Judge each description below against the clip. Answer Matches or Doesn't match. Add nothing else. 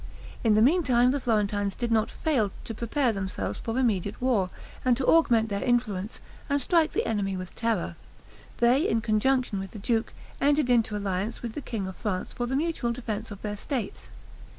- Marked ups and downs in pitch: Doesn't match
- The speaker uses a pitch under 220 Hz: Doesn't match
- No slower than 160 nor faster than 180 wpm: Doesn't match